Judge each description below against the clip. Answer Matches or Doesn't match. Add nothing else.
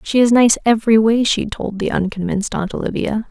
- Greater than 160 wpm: Matches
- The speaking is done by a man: Doesn't match